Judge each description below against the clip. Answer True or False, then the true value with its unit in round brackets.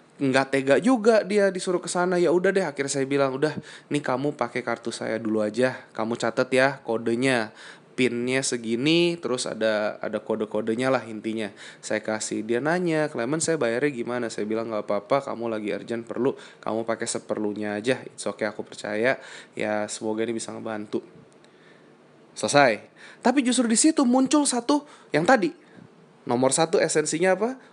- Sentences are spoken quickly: True (165 wpm)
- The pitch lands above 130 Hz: False (125 Hz)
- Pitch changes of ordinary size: False (6.4 semitones)